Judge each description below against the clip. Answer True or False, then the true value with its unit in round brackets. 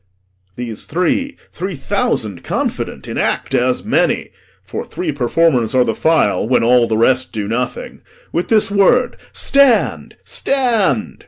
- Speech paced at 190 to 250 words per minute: False (140 wpm)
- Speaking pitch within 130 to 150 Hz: True (135 Hz)